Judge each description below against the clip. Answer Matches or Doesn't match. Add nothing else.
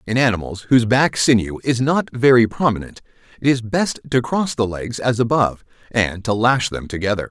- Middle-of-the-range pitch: Doesn't match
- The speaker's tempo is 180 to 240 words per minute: Matches